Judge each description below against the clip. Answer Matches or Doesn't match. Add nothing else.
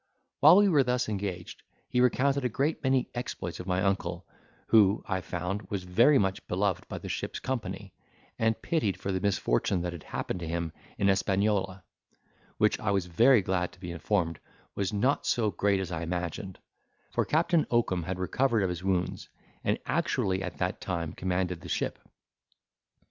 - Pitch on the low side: Matches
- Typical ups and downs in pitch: Matches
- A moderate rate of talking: Matches